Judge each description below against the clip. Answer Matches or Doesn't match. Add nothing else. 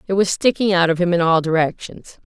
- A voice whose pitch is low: Doesn't match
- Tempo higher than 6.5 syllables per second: Doesn't match